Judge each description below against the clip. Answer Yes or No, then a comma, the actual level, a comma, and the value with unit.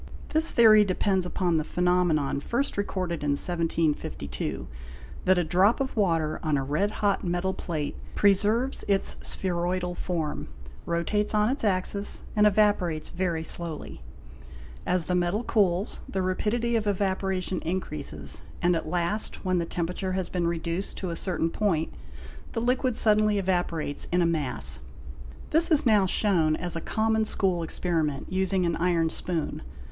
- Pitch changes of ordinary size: Yes, average, 3.6 semitones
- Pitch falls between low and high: Yes, medium, 180 Hz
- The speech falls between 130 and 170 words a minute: Yes, average, 150 wpm